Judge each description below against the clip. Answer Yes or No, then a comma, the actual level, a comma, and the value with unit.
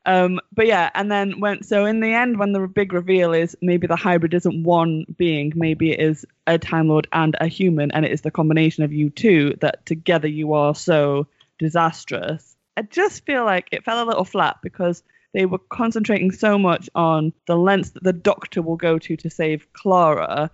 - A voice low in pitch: No, medium, 170 Hz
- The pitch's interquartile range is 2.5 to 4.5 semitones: Yes, average, 3.5 semitones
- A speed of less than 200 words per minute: No, fast, 205 wpm